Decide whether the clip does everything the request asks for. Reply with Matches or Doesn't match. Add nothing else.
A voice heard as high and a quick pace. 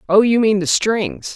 Matches